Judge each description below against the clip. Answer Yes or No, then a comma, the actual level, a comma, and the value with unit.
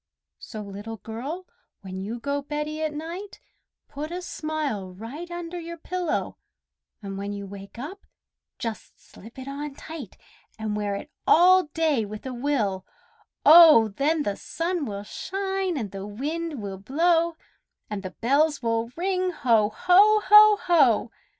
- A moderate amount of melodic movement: No, wide, 7.8 semitones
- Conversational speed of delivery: Yes, average, 150 wpm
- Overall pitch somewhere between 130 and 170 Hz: No, very high, 285 Hz